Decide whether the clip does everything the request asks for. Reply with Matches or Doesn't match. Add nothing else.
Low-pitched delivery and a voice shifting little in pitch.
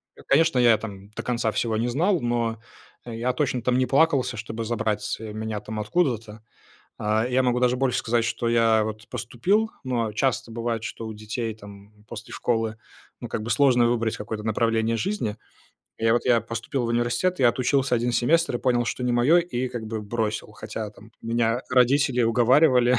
Matches